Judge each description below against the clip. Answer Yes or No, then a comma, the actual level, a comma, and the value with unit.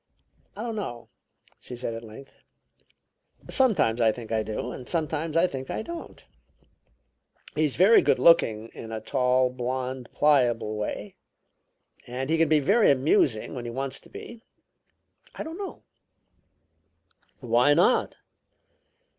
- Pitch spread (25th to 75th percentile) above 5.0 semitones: Yes, wide, 5.6 semitones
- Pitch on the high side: No, low, 130 Hz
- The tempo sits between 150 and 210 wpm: No, average, 140 wpm